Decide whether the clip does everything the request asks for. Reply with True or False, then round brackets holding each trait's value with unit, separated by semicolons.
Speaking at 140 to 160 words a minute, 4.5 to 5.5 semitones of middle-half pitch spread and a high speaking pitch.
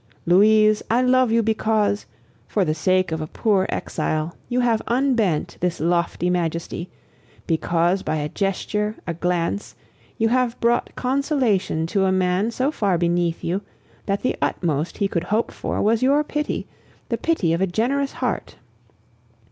True (155 wpm; 5.2 semitones; 200 Hz)